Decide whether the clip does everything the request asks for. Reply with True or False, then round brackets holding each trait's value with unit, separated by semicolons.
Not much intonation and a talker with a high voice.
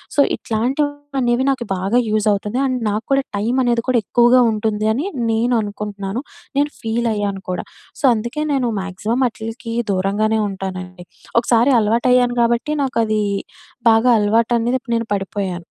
False (3.0 semitones; 225 Hz)